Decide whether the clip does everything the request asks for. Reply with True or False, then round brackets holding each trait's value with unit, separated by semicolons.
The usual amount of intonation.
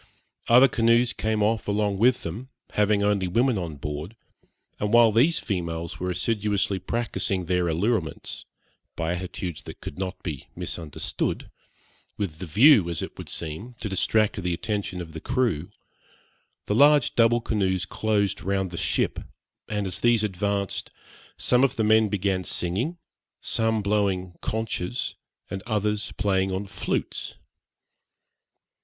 True (3.6 semitones)